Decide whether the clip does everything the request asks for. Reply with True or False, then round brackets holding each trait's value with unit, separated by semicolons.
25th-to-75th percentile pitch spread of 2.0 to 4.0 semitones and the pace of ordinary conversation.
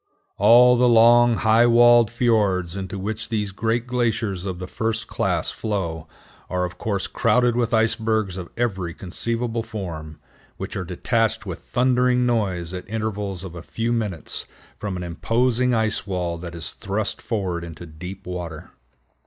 False (4.4 semitones; 155 wpm)